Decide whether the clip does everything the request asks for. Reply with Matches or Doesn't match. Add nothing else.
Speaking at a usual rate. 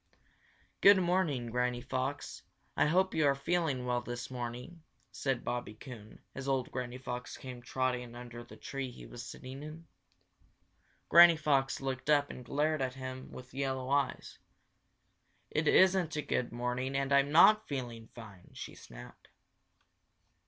Matches